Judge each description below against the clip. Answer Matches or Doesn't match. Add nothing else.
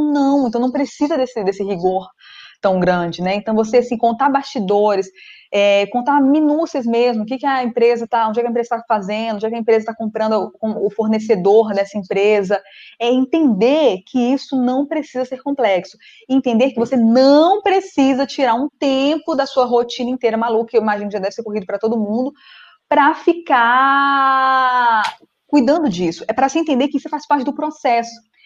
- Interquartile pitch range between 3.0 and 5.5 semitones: Matches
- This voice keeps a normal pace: Doesn't match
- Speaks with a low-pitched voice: Doesn't match